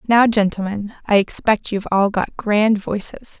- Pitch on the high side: Yes, high, 210 Hz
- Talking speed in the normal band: Yes, average, 160 wpm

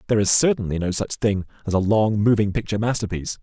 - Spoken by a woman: No, male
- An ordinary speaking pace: No, fast, 210 wpm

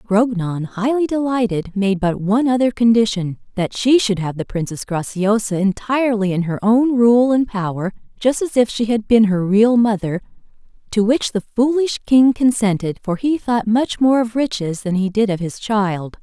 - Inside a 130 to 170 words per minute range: No, average, 180 wpm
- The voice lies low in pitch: No, high, 215 Hz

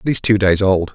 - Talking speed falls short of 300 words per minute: No, fast, 445 wpm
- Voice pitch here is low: Yes, low, 100 Hz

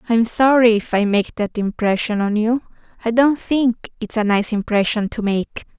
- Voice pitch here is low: No, high, 225 Hz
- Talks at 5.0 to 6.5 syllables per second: No, 4.8 syllables/s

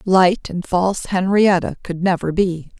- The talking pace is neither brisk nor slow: Yes, average, 150 wpm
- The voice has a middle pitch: Yes, medium, 180 Hz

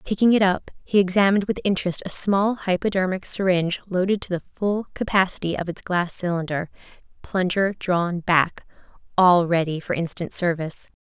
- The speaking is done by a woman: Yes, female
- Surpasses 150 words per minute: No, average, 145 wpm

